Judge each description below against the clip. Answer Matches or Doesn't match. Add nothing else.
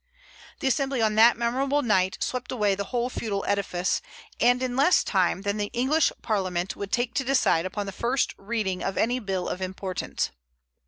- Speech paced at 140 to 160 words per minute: Doesn't match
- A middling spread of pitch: Matches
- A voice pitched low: Doesn't match